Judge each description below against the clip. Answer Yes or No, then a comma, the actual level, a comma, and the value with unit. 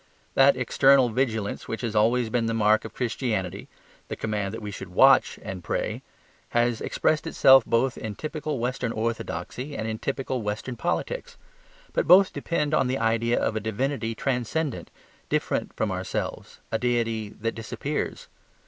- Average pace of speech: Yes, average, 155 wpm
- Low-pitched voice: Yes, low, 115 Hz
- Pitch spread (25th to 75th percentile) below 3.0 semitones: No, average, 3.4 semitones